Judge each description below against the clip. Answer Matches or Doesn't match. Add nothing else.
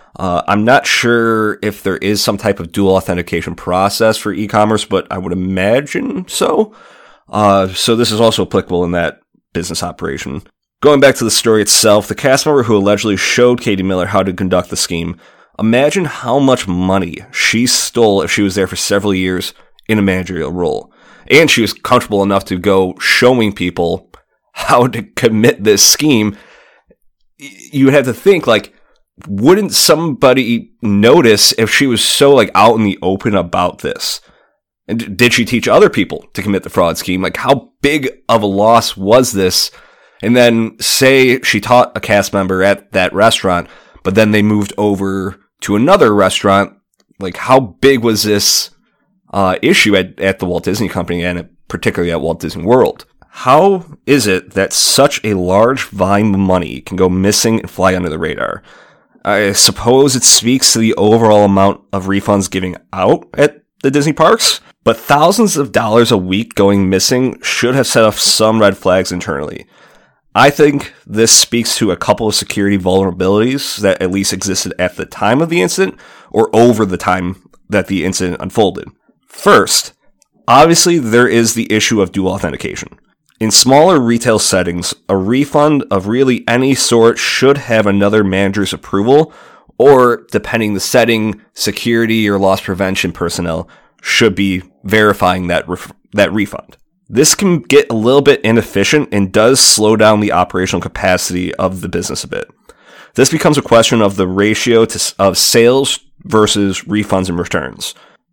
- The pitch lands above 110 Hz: Doesn't match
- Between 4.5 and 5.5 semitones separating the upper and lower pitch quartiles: Doesn't match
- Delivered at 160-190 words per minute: Matches